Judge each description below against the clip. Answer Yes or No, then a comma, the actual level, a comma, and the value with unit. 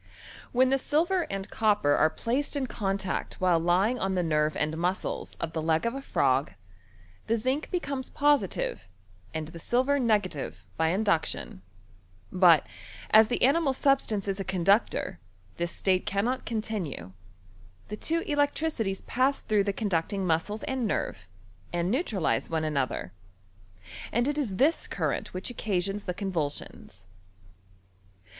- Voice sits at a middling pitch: No, high, 200 Hz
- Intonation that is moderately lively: No, wide, 7.3 semitones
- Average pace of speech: Yes, average, 150 wpm